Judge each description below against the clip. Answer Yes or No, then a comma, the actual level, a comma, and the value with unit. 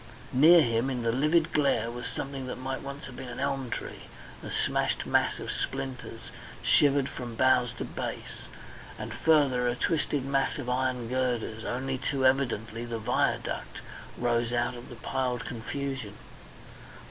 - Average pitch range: No, narrow, 2.3 semitones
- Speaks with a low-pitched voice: Yes, low, 130 Hz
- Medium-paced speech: Yes, average, 160 wpm